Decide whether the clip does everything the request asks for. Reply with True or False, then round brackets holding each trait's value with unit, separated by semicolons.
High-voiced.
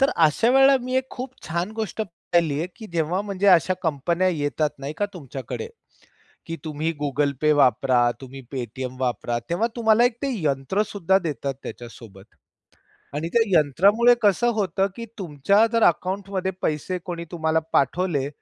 False (170 Hz)